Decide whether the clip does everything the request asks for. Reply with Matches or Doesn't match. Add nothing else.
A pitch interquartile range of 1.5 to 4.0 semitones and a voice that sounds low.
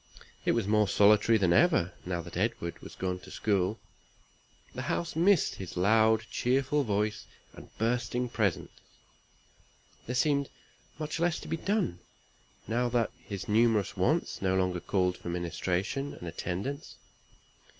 Doesn't match